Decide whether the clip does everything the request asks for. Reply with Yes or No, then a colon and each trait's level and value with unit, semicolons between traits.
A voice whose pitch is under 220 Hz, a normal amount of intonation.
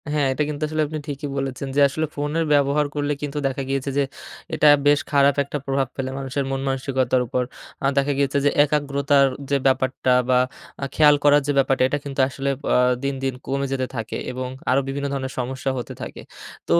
No: medium, 140 Hz; narrow, 1.5 semitones